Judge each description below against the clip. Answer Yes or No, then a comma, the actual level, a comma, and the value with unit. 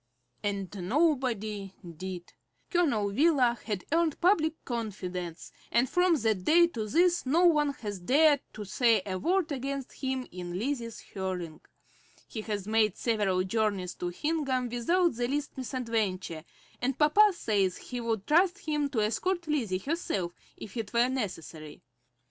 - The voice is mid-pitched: No, high, 235 Hz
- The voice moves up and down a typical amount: No, wide, 7.2 semitones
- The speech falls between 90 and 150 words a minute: Yes, average, 145 wpm